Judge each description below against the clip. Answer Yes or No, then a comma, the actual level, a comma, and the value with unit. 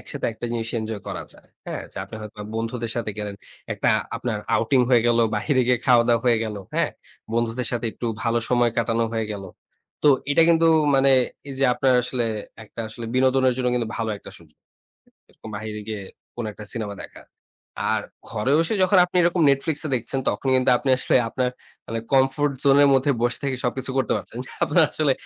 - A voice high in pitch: No, low, 120 Hz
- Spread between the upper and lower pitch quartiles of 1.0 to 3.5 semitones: Yes, average, 2.9 semitones